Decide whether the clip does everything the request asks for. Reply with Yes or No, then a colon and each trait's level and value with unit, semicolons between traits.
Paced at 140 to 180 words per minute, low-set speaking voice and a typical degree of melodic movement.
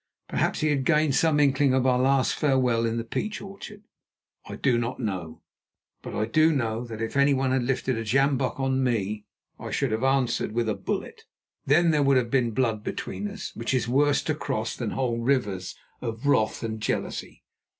No: average, 195 wpm; low, 130 Hz; average, 3.4 semitones